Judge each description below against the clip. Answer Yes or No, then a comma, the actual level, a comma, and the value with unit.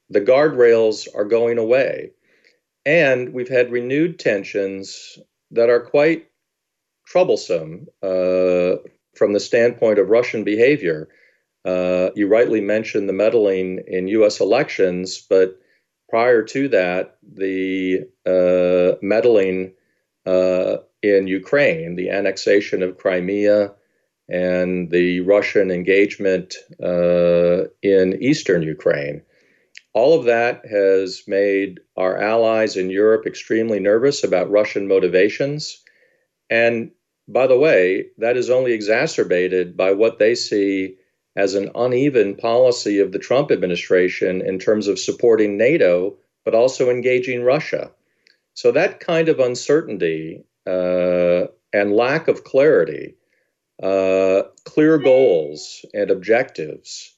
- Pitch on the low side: Yes, low, 105 Hz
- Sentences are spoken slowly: Yes, slow, 115 wpm